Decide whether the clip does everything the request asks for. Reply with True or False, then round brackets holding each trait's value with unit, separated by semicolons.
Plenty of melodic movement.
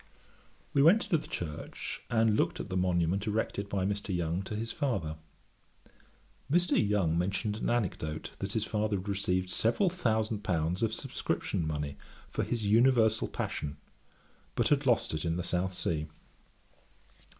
False (4.2 semitones)